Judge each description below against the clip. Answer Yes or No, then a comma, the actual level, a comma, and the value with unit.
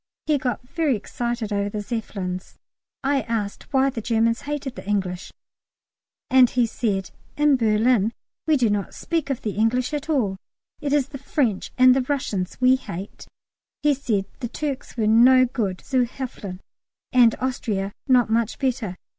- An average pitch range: Yes, average, 4.1 semitones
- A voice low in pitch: No, high, 240 Hz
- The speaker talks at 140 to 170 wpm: Yes, average, 165 wpm